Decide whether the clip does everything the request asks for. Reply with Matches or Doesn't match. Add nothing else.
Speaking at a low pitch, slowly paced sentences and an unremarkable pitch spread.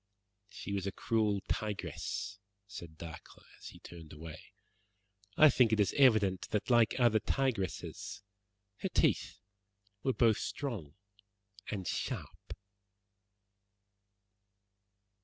Matches